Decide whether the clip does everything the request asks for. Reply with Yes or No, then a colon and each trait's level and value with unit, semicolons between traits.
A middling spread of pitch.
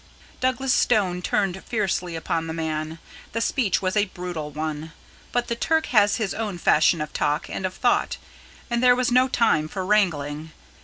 No: wide, 6.5 semitones